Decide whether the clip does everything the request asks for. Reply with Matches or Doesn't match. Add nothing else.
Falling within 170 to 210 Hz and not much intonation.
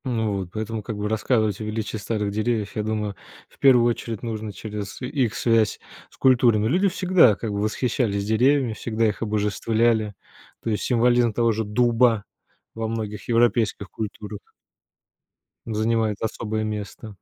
Doesn't match